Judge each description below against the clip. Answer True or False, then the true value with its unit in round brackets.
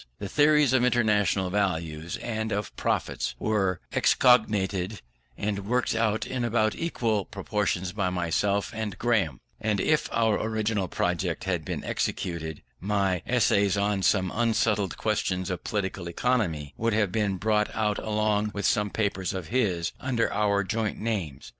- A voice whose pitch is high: False (105 Hz)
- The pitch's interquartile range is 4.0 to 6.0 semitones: False (2.9 semitones)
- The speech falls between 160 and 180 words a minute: False (145 wpm)